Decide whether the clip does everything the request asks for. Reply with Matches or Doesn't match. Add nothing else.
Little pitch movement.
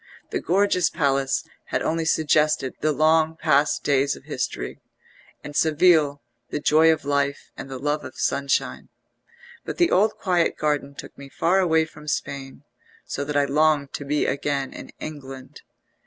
Matches